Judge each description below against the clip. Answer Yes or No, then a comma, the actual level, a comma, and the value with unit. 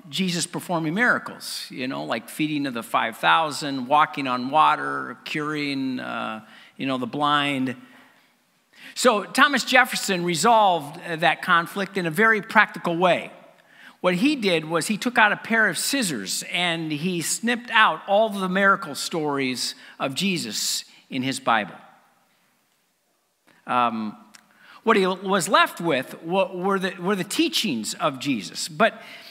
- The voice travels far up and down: Yes, wide, 6.3 semitones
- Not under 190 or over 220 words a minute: No, average, 140 wpm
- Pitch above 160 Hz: Yes, medium, 185 Hz